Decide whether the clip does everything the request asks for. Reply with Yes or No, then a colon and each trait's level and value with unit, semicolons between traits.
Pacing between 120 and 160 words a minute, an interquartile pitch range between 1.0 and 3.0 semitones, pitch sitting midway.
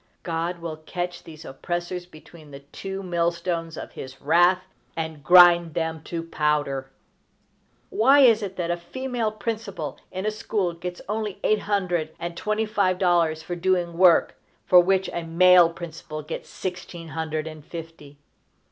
Yes: average, 155 wpm; narrow, 2.5 semitones; medium, 175 Hz